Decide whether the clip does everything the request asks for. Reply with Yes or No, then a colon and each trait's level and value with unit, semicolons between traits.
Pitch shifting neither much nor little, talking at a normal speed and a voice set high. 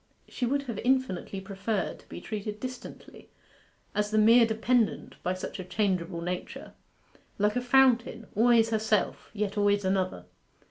Yes: average, 3.4 semitones; average, 145 wpm; high, 215 Hz